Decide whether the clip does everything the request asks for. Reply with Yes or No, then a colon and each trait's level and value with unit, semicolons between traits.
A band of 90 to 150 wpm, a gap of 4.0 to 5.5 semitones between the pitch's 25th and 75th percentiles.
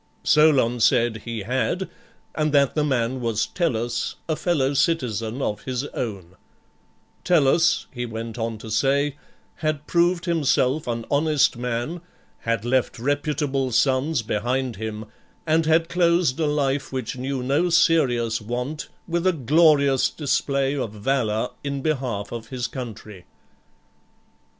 Yes: slow, 135 wpm; average, 4.6 semitones